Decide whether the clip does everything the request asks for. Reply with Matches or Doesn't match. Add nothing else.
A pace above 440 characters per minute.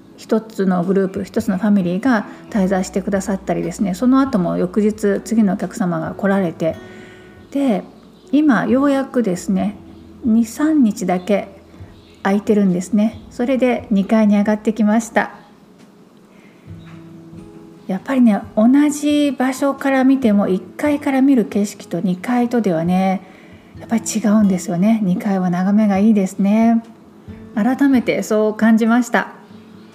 Doesn't match